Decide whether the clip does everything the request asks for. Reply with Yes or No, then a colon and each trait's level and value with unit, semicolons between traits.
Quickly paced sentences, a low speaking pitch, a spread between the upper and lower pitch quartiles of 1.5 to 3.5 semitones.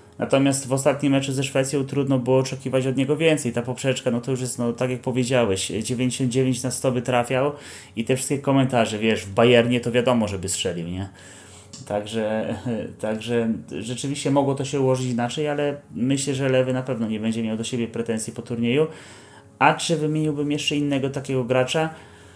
Yes: fast, 180 wpm; low, 130 Hz; average, 3.0 semitones